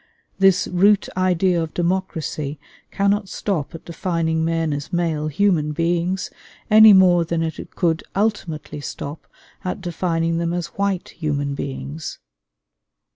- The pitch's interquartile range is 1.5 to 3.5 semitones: Yes, average, 3.0 semitones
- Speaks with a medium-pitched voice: Yes, medium, 170 Hz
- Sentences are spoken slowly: Yes, slow, 130 wpm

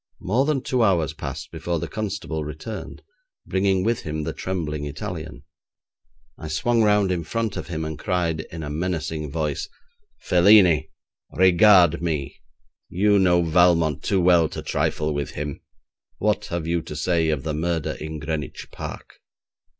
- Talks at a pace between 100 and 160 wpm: Yes, average, 155 wpm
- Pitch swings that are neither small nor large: Yes, average, 3.4 semitones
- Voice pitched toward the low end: Yes, very low, 85 Hz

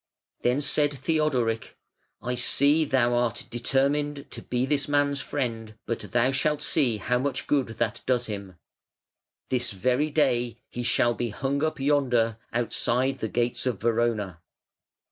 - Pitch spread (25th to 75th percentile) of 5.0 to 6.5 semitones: No, average, 3.2 semitones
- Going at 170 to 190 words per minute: No, average, 145 wpm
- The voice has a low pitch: Yes, low, 125 Hz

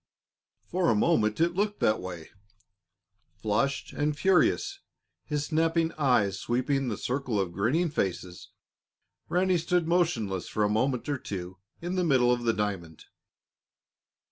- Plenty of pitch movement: Yes, wide, 8.1 semitones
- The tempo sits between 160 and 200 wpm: No, average, 140 wpm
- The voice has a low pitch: Yes, low, 130 Hz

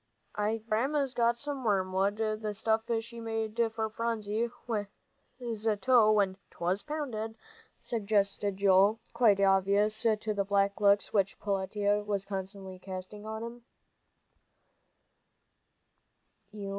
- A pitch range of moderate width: No, narrow, 2.1 semitones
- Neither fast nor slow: No, slow, 110 wpm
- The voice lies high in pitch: Yes, high, 210 Hz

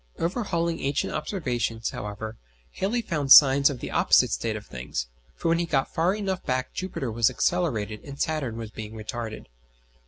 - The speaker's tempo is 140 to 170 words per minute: Yes, average, 165 wpm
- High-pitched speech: No, low, 135 Hz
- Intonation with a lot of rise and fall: Yes, wide, 7.1 semitones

